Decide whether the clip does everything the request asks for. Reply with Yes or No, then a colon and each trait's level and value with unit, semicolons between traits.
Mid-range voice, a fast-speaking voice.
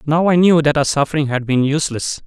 Yes: medium, 150 Hz; fast, 240 wpm